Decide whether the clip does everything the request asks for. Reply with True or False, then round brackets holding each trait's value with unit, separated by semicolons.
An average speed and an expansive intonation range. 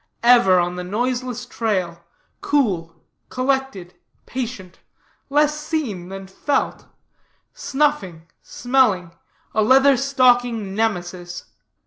False (90 wpm; 6.4 semitones)